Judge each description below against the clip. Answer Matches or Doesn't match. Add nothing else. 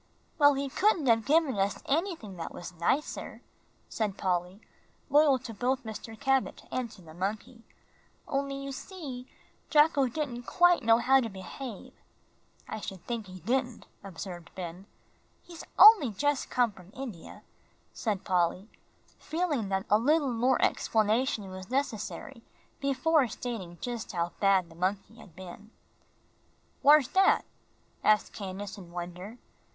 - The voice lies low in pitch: Doesn't match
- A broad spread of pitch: Matches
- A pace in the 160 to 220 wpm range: Doesn't match